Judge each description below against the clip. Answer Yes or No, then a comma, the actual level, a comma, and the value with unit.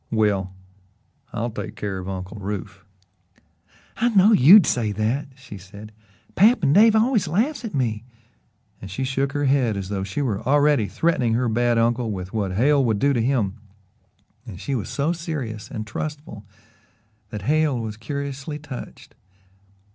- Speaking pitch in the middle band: No, low, 120 Hz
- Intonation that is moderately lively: No, wide, 5.7 semitones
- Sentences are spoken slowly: No, average, 160 wpm